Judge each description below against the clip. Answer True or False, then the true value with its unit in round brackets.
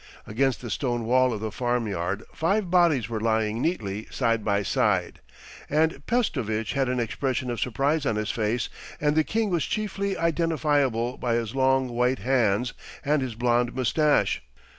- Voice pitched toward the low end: True (125 Hz)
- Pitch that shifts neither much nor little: True (4.8 semitones)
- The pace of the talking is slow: False (165 wpm)